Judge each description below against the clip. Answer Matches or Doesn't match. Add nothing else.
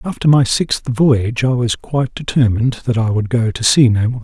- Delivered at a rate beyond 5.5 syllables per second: Doesn't match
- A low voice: Matches